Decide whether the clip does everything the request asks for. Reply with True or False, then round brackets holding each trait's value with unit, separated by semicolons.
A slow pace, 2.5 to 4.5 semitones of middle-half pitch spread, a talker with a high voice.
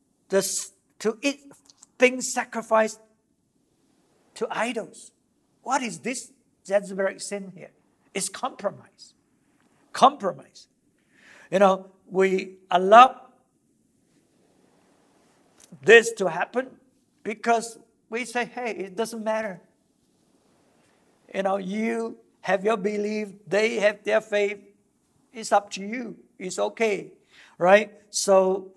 True (100 wpm; 3.5 semitones; 215 Hz)